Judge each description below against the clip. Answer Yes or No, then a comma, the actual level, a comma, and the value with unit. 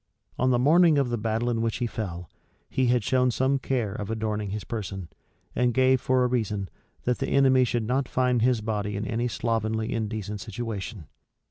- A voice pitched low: Yes, low, 115 Hz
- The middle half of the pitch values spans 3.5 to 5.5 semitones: No, average, 3.0 semitones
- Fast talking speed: No, average, 195 wpm